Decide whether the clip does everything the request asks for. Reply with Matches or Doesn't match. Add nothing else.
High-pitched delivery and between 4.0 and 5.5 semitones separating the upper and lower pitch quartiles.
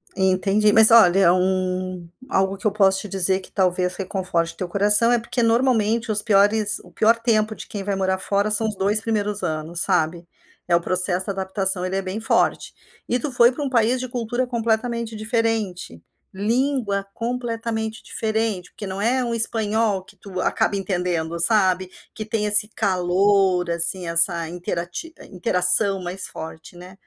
Doesn't match